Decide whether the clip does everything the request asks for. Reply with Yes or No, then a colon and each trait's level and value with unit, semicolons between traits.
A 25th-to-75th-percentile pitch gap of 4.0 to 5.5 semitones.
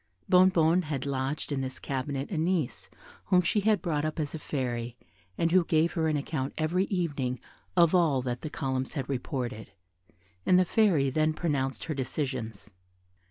Yes: average, 4.3 semitones